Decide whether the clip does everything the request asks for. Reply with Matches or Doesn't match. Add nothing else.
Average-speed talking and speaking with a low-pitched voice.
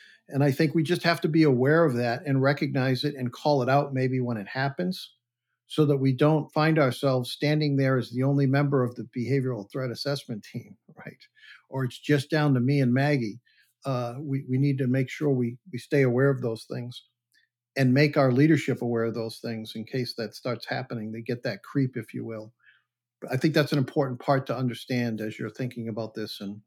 Doesn't match